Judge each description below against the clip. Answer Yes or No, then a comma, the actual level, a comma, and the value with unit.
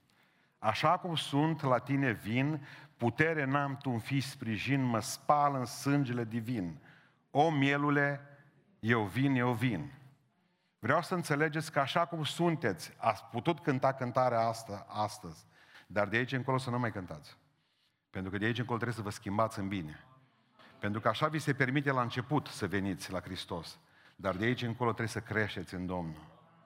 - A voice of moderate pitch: No, low, 125 Hz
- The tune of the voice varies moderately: Yes, average, 4.6 semitones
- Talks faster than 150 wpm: Yes, fast, 170 wpm